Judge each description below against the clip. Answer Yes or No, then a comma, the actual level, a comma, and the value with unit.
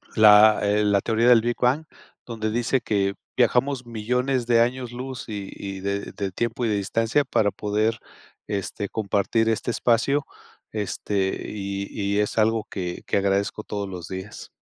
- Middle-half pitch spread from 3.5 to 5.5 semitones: No, average, 2.8 semitones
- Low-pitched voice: Yes, low, 110 Hz